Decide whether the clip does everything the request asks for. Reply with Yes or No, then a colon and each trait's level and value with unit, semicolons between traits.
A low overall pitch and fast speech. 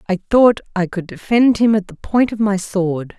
No: high, 200 Hz; fast, 225 wpm